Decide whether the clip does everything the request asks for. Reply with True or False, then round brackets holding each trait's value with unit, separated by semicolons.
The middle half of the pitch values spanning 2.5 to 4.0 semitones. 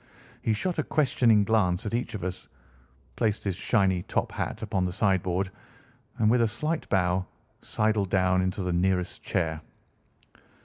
True (3.3 semitones)